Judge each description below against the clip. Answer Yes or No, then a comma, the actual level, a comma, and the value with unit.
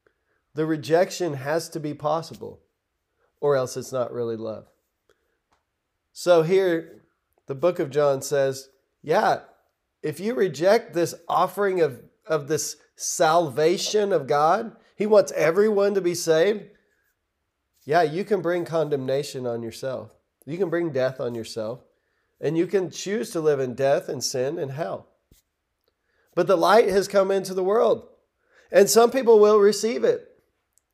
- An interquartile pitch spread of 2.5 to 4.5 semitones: No, wide, 5.6 semitones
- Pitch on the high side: No, medium, 175 Hz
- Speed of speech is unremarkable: Yes, average, 145 wpm